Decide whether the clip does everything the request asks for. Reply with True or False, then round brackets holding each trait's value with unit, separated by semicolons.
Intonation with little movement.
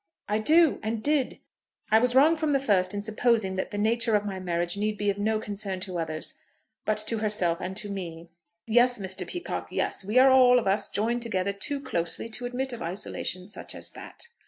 False (4.3 semitones)